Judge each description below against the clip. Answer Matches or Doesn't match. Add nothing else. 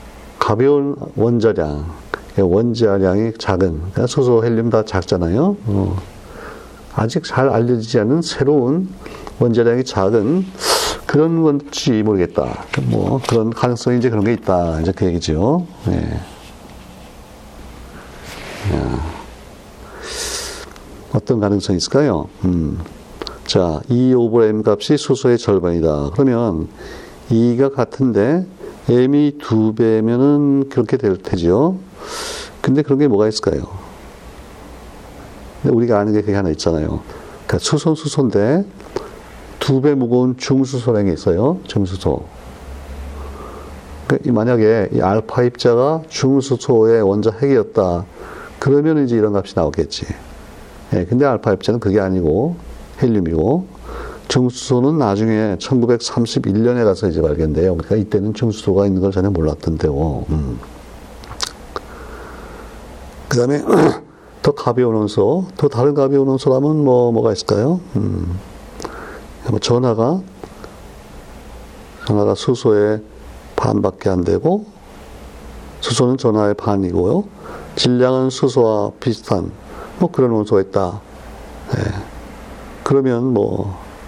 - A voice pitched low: Matches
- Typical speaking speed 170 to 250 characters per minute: Matches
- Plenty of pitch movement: Matches